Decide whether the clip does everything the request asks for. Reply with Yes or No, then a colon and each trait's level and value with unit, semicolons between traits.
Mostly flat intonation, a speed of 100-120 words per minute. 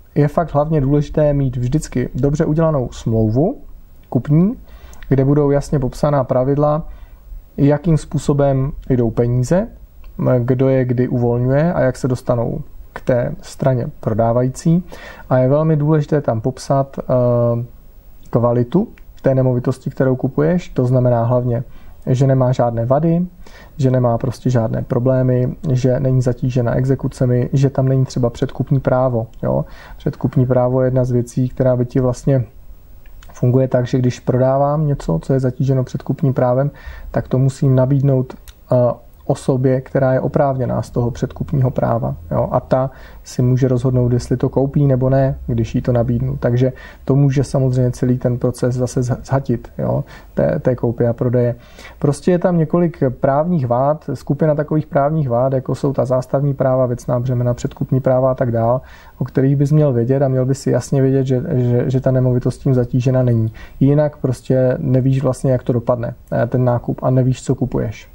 No: narrow, 2.0 semitones; average, 160 wpm